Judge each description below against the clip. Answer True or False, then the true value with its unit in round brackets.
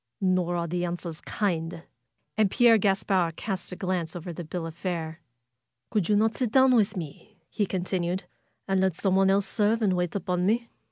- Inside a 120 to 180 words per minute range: False (190 wpm)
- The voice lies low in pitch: False (185 Hz)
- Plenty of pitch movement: False (2.9 semitones)